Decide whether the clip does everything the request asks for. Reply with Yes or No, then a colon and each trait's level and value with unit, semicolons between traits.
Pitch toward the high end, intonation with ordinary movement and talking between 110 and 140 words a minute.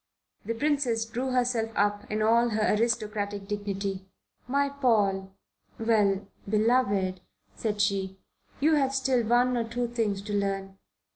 Yes: high, 220 Hz; average, 3.3 semitones; slow, 135 wpm